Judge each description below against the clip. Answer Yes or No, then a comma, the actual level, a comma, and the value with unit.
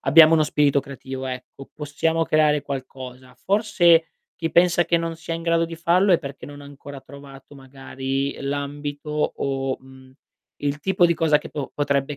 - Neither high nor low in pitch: Yes, medium, 145 Hz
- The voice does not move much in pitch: No, average, 3.2 semitones